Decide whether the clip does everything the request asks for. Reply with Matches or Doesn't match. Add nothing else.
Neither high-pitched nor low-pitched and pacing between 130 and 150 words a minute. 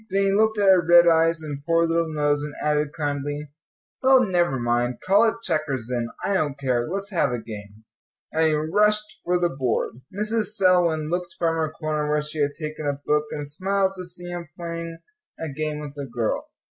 Doesn't match